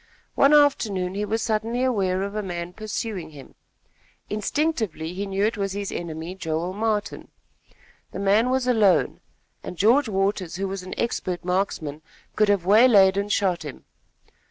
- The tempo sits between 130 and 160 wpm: Yes, average, 155 wpm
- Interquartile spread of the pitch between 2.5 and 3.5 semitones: Yes, average, 3.2 semitones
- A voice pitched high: Yes, high, 200 Hz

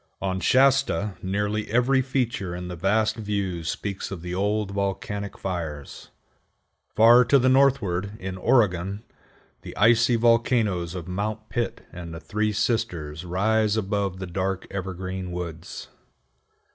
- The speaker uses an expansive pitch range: No, average, 3.4 semitones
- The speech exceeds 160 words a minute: No, slow, 135 wpm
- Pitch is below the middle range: Yes, low, 100 Hz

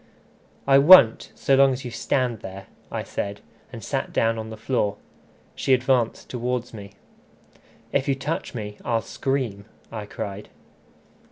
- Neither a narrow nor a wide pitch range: Yes, average, 4.1 semitones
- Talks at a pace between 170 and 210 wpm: No, average, 150 wpm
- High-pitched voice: No, low, 120 Hz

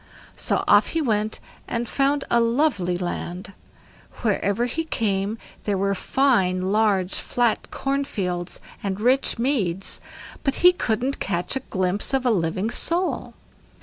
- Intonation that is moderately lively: No, wide, 5.8 semitones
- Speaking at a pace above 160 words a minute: No, average, 140 wpm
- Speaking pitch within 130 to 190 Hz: No, high, 220 Hz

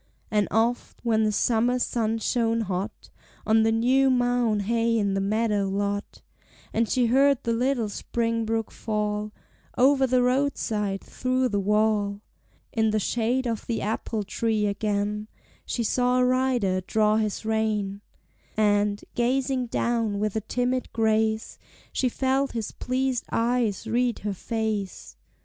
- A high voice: Yes, high, 225 Hz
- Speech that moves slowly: No, average, 145 wpm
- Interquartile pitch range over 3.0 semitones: No, average, 2.7 semitones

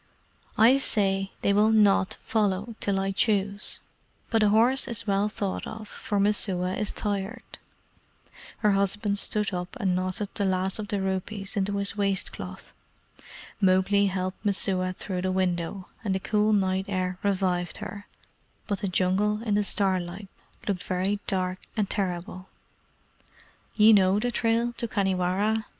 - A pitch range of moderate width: No, narrow, 2.0 semitones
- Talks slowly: No, average, 150 wpm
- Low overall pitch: No, high, 200 Hz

